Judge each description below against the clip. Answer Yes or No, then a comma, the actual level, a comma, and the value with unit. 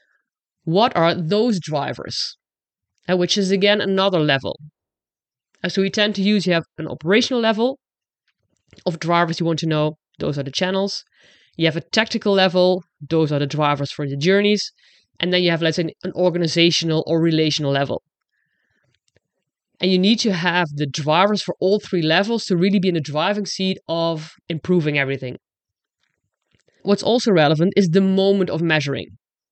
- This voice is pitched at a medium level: Yes, medium, 175 Hz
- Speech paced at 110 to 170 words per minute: Yes, average, 165 wpm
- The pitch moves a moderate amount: Yes, average, 3.9 semitones